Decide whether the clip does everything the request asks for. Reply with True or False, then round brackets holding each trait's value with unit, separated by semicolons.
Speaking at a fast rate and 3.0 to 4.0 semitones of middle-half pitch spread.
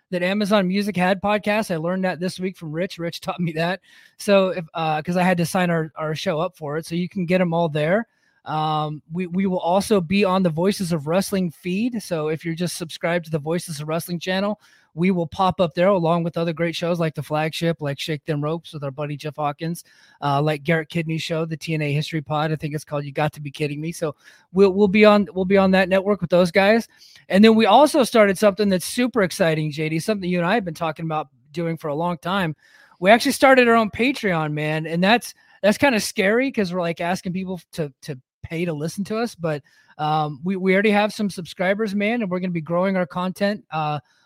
True (245 wpm; 3.6 semitones)